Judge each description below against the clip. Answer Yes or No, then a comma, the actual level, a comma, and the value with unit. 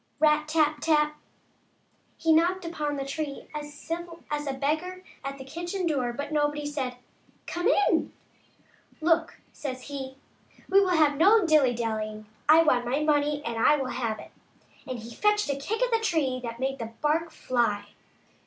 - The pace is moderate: Yes, average, 185 wpm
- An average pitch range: Yes, average, 3.7 semitones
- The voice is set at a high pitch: Yes, very high, 295 Hz